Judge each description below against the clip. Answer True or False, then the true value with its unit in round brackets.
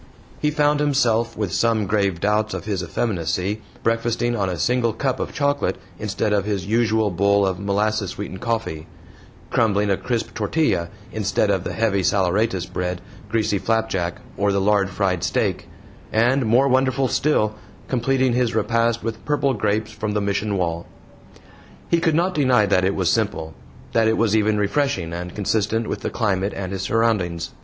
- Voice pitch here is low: True (105 Hz)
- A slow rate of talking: False (170 wpm)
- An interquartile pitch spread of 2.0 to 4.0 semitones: True (3.1 semitones)